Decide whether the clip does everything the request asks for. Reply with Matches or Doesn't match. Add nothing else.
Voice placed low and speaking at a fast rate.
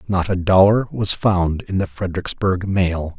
Doesn't match